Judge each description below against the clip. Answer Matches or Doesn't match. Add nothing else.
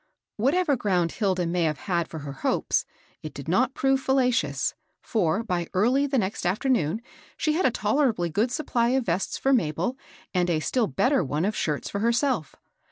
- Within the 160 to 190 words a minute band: Matches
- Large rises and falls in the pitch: Matches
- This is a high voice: Matches